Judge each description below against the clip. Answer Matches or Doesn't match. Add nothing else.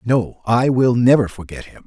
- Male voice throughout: Matches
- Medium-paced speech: Matches